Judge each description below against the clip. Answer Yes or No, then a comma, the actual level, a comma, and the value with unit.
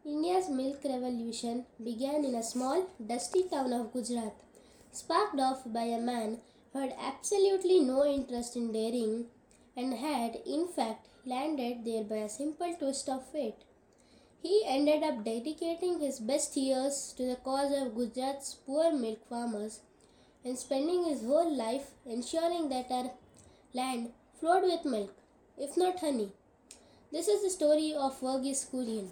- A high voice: Yes, very high, 265 Hz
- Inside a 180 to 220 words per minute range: No, average, 150 wpm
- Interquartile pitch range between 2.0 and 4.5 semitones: Yes, average, 3.9 semitones